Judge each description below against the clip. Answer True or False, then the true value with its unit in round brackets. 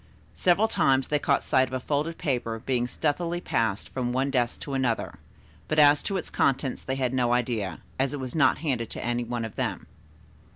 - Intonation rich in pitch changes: False (3.2 semitones)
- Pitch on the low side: True (130 Hz)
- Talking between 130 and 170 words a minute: False (205 wpm)